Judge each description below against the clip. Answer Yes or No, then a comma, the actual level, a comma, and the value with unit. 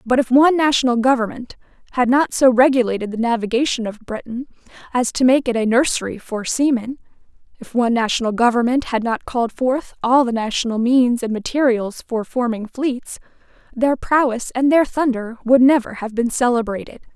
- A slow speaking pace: No, average, 165 wpm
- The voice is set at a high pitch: Yes, high, 245 Hz